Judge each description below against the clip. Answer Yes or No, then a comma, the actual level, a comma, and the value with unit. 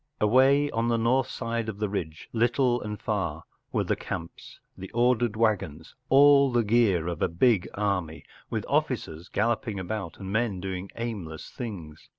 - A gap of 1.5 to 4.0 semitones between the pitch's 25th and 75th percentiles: No, average, 4.5 semitones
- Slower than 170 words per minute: Yes, average, 160 wpm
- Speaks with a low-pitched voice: Yes, low, 110 Hz